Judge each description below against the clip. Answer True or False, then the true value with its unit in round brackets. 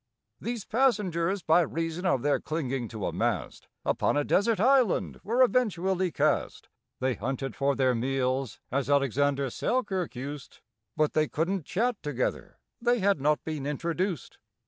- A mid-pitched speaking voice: True (155 Hz)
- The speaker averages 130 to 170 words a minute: True (145 wpm)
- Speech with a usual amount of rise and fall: False (6.2 semitones)